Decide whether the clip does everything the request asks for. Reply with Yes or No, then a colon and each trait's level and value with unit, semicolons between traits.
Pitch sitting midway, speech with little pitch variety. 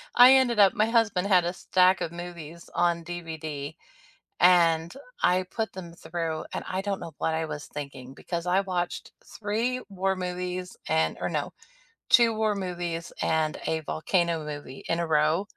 No: medium, 175 Hz; average, 3.1 semitones